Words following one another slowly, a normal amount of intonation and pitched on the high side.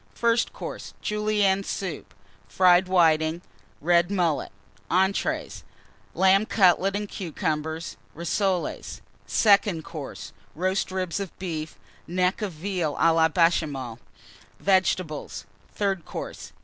No: slow, 105 wpm; average, 3.2 semitones; medium, 180 Hz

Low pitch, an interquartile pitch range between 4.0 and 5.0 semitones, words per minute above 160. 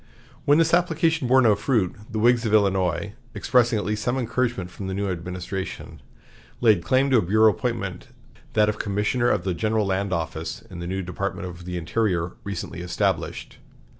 Yes: low, 105 Hz; average, 4.7 semitones; average, 180 wpm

